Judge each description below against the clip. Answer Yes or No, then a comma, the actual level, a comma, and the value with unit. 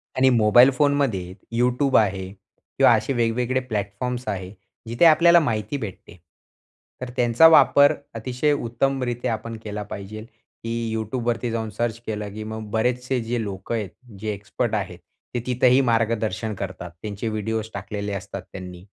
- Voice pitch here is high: No, low, 115 Hz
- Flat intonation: No, average, 3.0 semitones